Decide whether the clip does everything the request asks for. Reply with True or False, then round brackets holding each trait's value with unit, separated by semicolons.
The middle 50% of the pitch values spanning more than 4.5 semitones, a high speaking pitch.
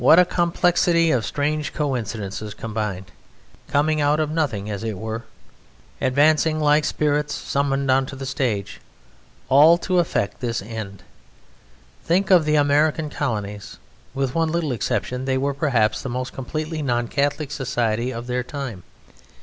False (4.9 semitones; 135 Hz)